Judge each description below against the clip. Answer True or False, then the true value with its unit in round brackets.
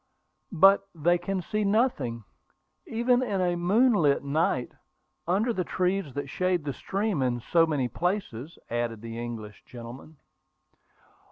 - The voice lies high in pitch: False (170 Hz)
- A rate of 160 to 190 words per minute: False (135 wpm)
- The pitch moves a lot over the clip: True (7.5 semitones)